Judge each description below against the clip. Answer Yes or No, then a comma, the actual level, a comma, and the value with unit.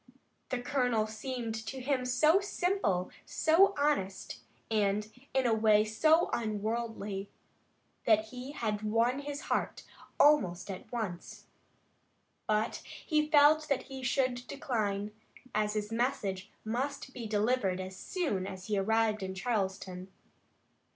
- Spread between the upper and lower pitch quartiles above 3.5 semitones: Yes, average, 4.5 semitones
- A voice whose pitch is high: Yes, high, 225 Hz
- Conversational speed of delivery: No, slow, 125 wpm